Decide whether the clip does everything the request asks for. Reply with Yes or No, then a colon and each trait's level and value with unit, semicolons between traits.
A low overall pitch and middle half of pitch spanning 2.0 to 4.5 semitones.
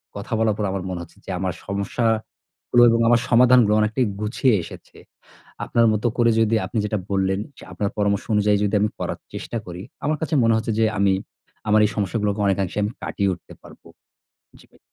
Yes: low, 105 Hz; narrow, 2.5 semitones